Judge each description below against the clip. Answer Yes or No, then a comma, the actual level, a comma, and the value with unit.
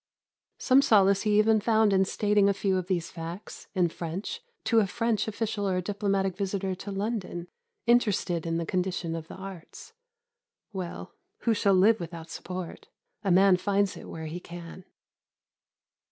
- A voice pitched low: No, high, 195 Hz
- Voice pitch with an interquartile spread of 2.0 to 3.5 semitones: Yes, average, 2.8 semitones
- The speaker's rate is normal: Yes, average, 160 wpm